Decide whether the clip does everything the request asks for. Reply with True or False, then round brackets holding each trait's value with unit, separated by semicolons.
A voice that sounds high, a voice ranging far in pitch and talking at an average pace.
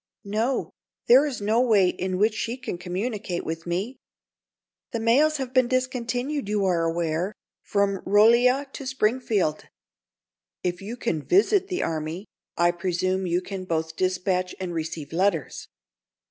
True (200 Hz; 5.7 semitones; 145 wpm)